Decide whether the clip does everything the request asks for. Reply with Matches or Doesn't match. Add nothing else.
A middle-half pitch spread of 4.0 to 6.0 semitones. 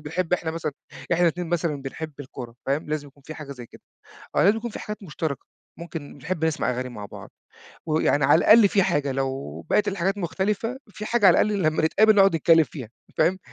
Matches